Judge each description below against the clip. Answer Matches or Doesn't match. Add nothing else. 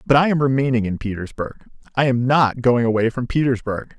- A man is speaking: Matches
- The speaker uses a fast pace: Doesn't match